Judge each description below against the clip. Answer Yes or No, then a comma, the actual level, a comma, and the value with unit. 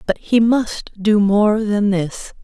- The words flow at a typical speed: Yes, average, 170 wpm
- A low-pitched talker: No, high, 210 Hz